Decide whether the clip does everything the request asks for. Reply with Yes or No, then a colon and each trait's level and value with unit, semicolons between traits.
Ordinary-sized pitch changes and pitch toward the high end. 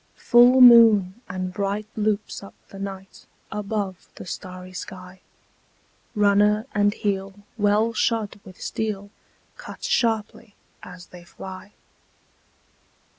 No: narrow, 2.3 semitones; high, 205 Hz